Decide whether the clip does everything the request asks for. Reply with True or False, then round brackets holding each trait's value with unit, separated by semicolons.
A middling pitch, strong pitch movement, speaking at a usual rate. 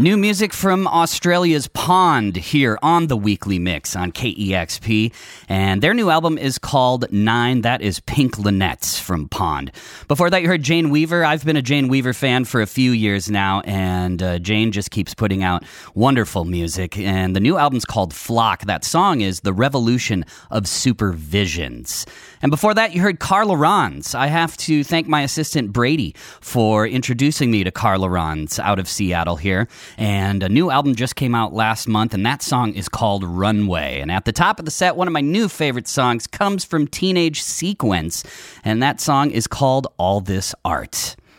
False (115 Hz; 7.1 semitones; 185 wpm)